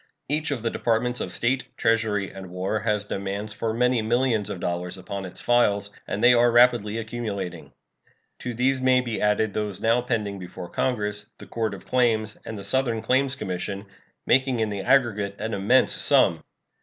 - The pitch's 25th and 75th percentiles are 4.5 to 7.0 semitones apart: No, average, 3.4 semitones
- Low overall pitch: Yes, low, 110 Hz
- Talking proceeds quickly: No, average, 180 wpm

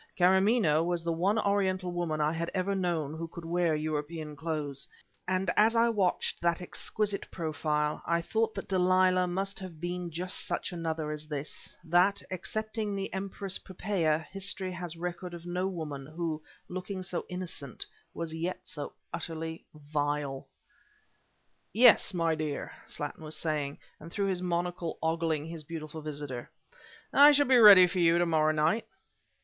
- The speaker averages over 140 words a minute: Yes, average, 155 wpm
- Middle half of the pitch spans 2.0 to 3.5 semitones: Yes, average, 3.1 semitones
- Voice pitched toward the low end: No, medium, 170 Hz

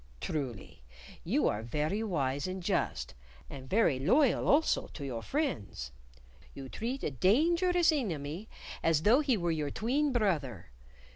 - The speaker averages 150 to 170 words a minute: No, average, 140 wpm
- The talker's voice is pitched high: No, medium, 175 Hz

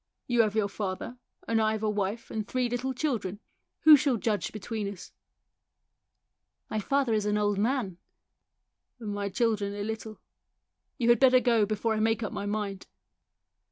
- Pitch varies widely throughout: No, average, 2.7 semitones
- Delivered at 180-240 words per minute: Yes, average, 190 wpm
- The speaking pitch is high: Yes, high, 215 Hz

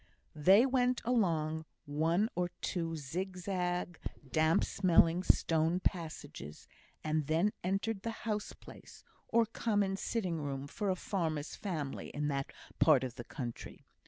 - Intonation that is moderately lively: Yes, average, 4.3 semitones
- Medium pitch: Yes, medium, 175 Hz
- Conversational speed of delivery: No, slow, 130 wpm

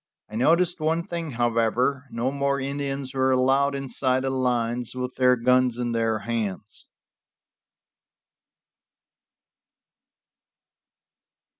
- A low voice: Yes, low, 130 Hz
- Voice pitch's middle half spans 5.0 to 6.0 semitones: No, average, 2.7 semitones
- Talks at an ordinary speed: No, slow, 100 wpm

